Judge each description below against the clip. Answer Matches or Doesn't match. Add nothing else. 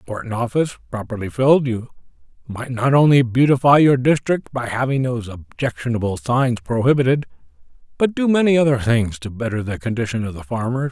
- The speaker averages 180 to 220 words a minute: Doesn't match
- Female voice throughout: Doesn't match